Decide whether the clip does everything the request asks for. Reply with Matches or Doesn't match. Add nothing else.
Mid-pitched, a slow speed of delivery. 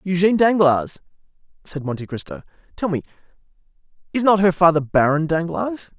Matches